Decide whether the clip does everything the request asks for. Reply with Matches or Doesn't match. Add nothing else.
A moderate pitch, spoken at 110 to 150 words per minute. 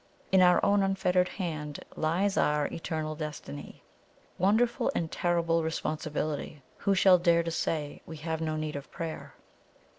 Matches